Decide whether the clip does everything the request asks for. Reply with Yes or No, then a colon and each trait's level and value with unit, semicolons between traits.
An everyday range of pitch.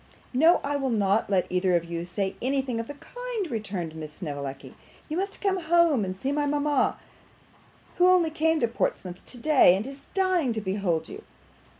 No: wide, 8.9 semitones